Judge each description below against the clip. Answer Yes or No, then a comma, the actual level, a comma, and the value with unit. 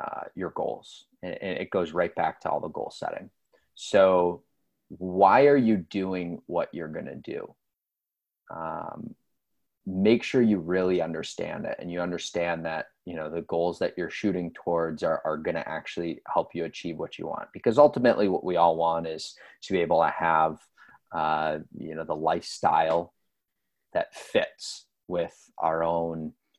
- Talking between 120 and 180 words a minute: Yes, average, 170 wpm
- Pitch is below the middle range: Yes, very low, 85 Hz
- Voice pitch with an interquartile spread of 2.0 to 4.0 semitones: Yes, narrow, 2.5 semitones